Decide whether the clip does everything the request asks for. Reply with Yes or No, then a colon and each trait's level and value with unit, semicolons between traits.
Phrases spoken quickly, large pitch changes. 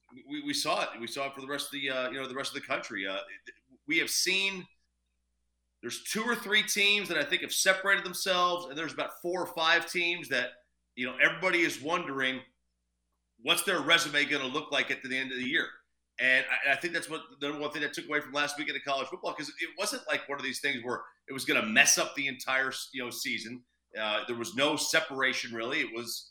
Yes: fast, 245 wpm; wide, 6.0 semitones